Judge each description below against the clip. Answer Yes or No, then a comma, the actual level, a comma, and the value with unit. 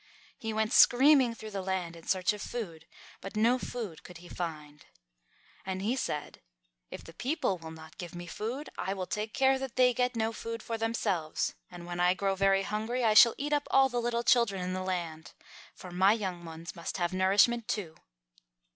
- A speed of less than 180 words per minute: No, average, 200 wpm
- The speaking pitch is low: No, high, 200 Hz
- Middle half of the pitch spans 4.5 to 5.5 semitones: Yes, average, 4.9 semitones